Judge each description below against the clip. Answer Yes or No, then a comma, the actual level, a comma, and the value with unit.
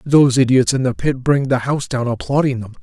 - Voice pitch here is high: No, low, 130 Hz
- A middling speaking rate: No, fast, 235 wpm